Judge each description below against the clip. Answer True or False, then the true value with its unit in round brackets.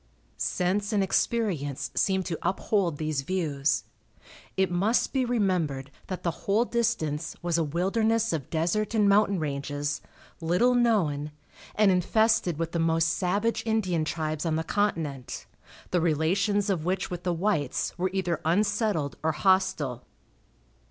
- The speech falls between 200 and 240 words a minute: False (140 wpm)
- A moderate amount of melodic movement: True (4.6 semitones)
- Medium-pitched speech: True (180 Hz)